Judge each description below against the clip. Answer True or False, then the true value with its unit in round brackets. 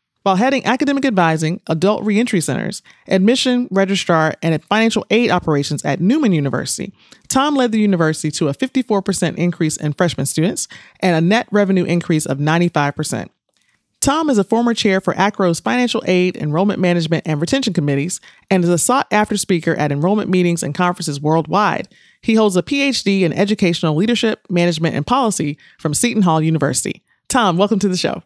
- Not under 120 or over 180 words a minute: True (170 wpm)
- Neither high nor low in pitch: True (180 Hz)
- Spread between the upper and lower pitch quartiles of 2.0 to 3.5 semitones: False (5.0 semitones)